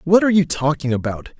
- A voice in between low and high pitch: Yes, medium, 155 Hz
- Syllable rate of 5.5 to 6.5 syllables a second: Yes, 6.3 syllables/s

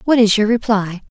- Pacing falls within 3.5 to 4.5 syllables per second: No, 5.4 syllables/s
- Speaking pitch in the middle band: No, high, 215 Hz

